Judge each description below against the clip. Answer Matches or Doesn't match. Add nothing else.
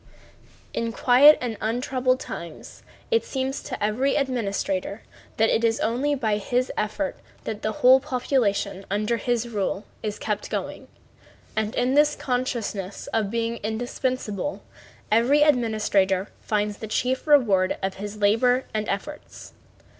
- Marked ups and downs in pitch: Doesn't match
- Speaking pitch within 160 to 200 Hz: Doesn't match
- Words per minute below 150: Matches